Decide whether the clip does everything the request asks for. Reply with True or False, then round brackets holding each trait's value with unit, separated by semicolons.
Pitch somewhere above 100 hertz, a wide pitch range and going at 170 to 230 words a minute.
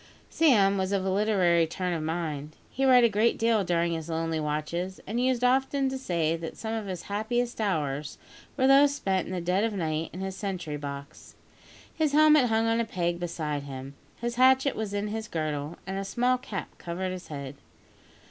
True (190 Hz; 6.1 semitones; 200 wpm)